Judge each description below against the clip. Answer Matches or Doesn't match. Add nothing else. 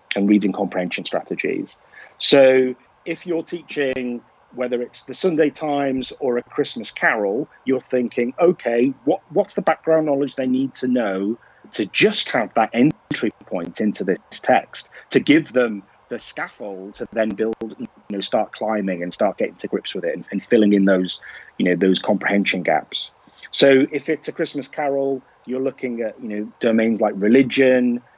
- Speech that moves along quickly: Doesn't match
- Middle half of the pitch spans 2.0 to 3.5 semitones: Doesn't match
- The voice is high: Doesn't match